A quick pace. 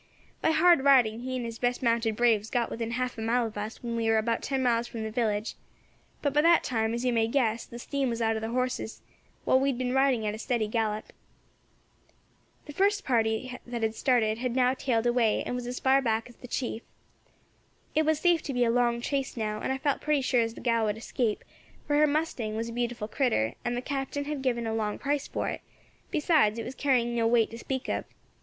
Yes: fast, 235 wpm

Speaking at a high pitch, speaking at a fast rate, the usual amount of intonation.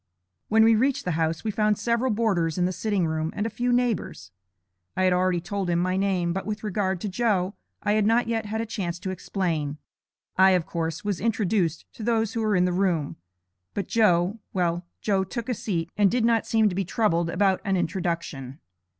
Yes: high, 195 Hz; fast, 210 wpm; average, 4.0 semitones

